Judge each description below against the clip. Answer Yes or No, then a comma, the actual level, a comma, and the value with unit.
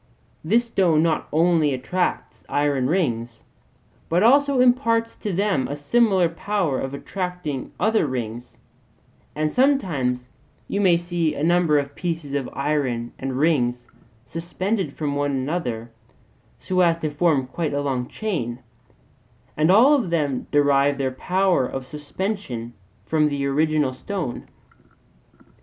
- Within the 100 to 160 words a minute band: Yes, slow, 135 wpm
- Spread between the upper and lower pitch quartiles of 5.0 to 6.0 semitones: Yes, average, 5.3 semitones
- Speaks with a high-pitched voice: No, medium, 155 Hz